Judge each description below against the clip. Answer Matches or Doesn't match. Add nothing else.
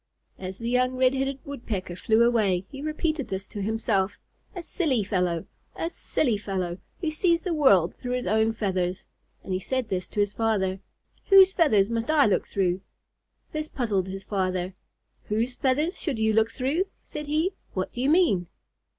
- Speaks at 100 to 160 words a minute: Doesn't match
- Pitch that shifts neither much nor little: Doesn't match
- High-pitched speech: Matches